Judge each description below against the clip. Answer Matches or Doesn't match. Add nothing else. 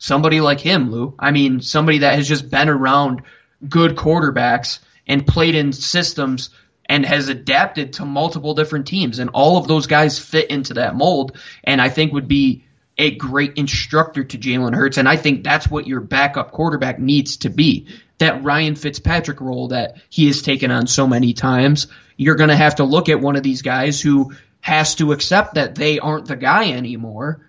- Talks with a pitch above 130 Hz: Matches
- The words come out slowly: Doesn't match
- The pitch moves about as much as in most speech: Doesn't match